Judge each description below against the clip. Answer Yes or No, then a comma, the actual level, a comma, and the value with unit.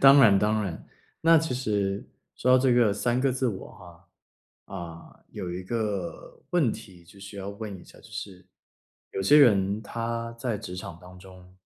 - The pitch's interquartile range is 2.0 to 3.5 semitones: No, average, 4.2 semitones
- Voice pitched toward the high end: No, low, 100 Hz